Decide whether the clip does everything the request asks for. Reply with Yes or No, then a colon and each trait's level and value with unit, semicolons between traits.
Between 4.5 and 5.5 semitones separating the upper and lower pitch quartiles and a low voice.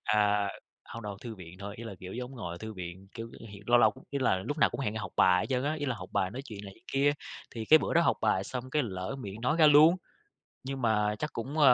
Yes: average, 5.2 semitones; low, 115 Hz